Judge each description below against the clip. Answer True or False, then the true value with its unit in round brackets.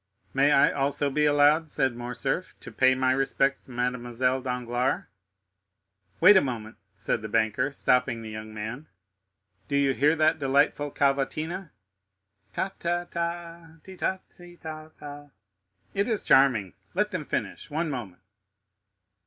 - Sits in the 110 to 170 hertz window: True (140 Hz)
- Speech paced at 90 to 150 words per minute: True (140 wpm)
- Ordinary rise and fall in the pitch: True (4.0 semitones)